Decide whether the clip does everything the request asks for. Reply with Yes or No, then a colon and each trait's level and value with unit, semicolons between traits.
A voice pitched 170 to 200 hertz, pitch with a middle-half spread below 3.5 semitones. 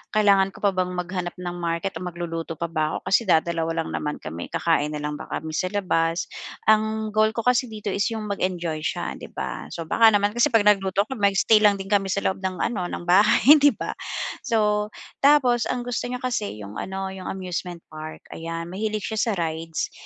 No: high, 190 Hz; average, 4.2 semitones